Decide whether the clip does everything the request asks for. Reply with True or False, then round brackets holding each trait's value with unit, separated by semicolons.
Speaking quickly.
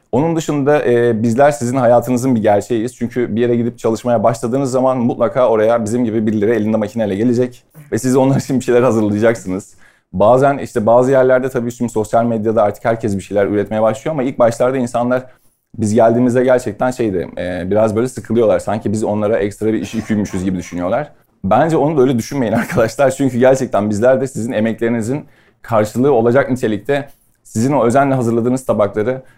True (175 wpm)